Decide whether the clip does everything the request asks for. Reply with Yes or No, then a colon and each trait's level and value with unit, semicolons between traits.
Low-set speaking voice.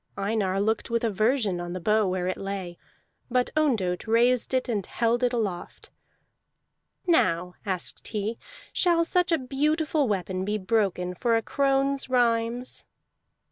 No: high, 225 Hz